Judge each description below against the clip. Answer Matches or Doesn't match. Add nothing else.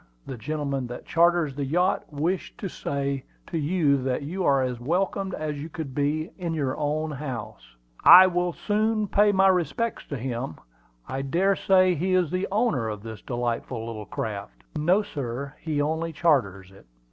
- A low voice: Doesn't match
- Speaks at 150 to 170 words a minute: Doesn't match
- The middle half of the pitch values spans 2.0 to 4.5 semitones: Doesn't match